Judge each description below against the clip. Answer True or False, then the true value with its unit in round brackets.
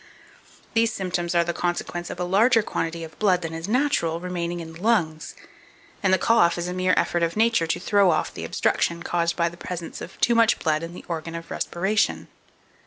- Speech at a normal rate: False (210 wpm)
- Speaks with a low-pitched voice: False (175 Hz)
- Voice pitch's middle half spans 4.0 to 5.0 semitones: False (3.0 semitones)